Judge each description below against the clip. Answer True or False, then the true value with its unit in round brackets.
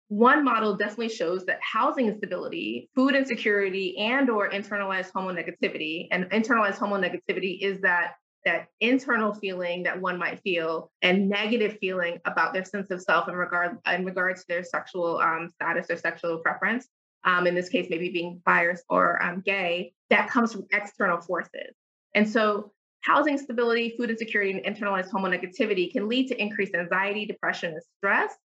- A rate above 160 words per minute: True (170 wpm)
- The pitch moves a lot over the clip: False (3.5 semitones)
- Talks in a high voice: True (195 Hz)